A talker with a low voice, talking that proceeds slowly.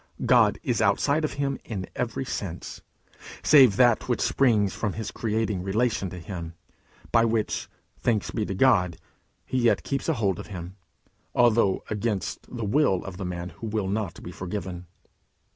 No: low, 105 Hz; average, 165 wpm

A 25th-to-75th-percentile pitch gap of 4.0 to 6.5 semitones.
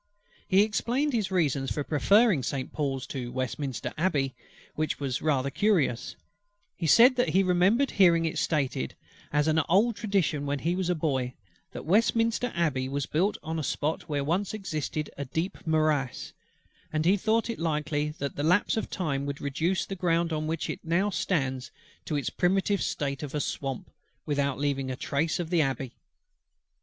Yes: average, 5.0 semitones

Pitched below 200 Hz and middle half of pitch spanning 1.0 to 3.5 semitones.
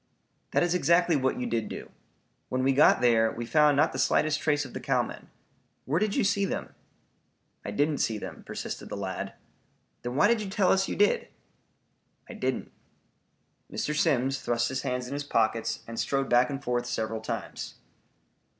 No: low, 135 Hz; average, 4.5 semitones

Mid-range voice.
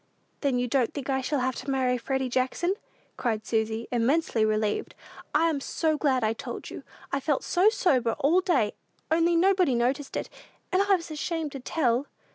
No: very high, 270 Hz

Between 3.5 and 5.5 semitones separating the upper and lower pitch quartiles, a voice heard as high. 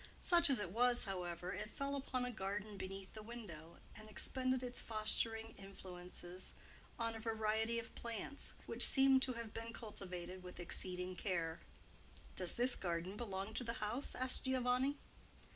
Yes: average, 4.7 semitones; high, 215 Hz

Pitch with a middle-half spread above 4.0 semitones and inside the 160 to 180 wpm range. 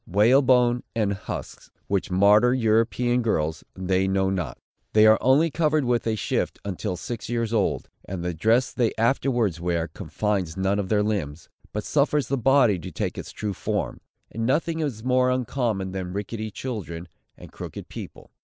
Yes: average, 4.4 semitones; average, 170 wpm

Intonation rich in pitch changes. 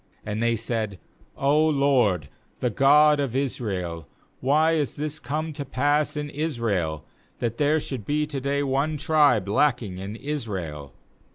Yes: wide, 5.7 semitones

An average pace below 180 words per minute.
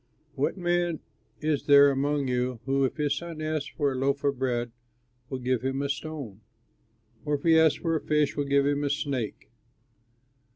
No: average, 195 wpm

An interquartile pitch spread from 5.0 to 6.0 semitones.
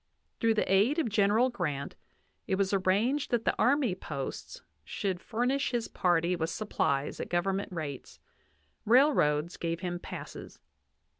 Yes: wide, 5.5 semitones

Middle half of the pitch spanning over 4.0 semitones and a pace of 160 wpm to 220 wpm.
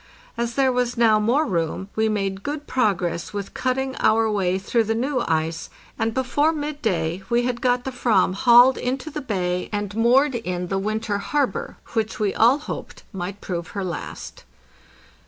Yes: average, 4.8 semitones; average, 175 wpm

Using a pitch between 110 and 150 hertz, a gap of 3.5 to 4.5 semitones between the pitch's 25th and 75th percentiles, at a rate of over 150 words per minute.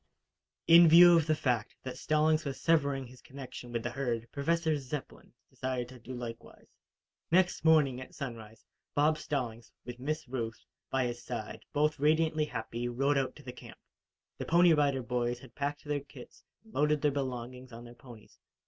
Yes: low, 135 Hz; average, 3.8 semitones; average, 175 wpm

